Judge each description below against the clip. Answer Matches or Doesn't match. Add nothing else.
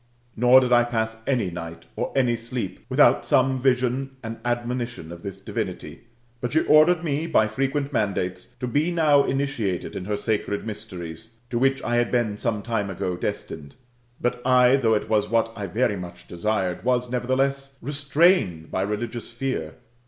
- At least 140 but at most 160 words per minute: Doesn't match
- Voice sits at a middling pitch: Doesn't match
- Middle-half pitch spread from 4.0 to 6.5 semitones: Matches